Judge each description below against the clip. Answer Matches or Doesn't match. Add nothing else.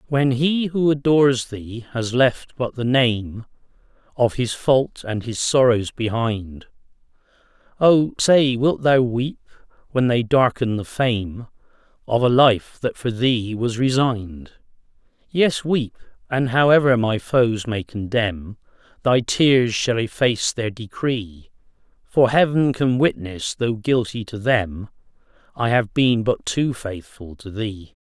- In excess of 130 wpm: Matches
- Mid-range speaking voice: Doesn't match